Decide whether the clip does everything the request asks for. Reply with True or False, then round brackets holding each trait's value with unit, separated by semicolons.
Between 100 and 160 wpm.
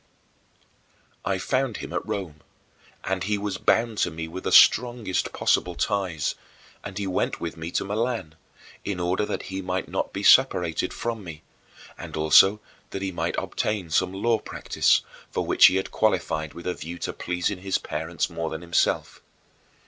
False (170 wpm)